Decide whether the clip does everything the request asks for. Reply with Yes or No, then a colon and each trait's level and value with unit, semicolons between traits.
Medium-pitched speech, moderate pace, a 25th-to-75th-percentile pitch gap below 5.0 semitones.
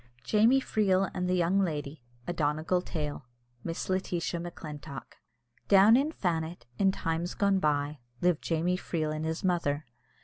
Yes: medium, 170 Hz; average, 150 wpm; average, 3.5 semitones